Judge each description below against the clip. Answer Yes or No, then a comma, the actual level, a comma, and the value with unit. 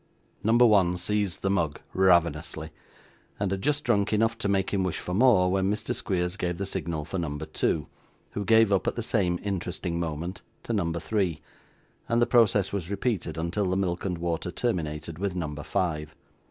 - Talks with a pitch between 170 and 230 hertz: No, very low, 95 Hz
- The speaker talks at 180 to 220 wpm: Yes, average, 185 wpm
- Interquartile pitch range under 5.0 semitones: Yes, average, 3.3 semitones